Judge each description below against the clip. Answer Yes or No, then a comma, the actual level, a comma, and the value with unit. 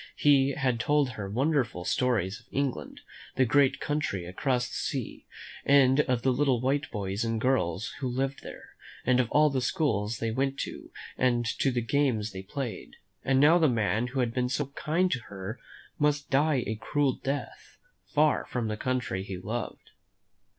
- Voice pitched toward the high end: No, low, 130 Hz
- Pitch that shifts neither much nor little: Yes, average, 3.9 semitones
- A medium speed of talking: Yes, average, 170 wpm